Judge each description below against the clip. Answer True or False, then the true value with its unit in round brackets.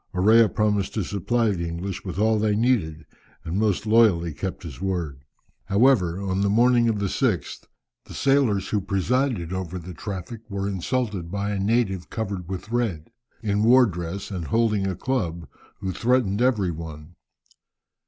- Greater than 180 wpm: False (165 wpm)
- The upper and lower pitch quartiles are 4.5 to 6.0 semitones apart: False (4.1 semitones)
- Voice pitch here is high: False (100 Hz)